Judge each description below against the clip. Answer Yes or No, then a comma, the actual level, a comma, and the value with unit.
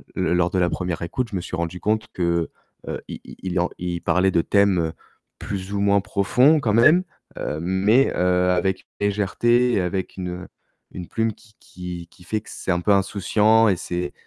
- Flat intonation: No, average, 3.0 semitones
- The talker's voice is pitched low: Yes, very low, 95 Hz